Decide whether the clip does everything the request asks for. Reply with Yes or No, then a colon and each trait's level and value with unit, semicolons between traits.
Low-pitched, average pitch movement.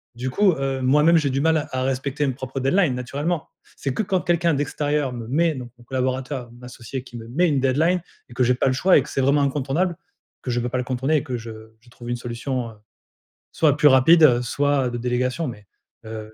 Yes: low, 130 Hz; average, 3.3 semitones